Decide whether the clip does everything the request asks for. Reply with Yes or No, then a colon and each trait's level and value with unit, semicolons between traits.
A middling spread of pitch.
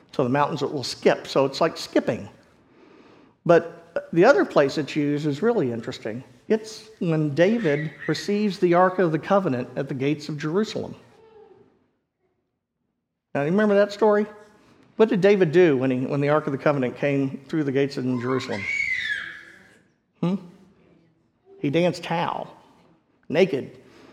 No: wide, 6.1 semitones